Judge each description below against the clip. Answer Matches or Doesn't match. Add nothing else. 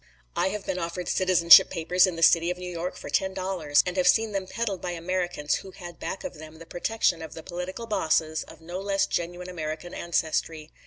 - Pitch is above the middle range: Doesn't match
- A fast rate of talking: Matches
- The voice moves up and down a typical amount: Doesn't match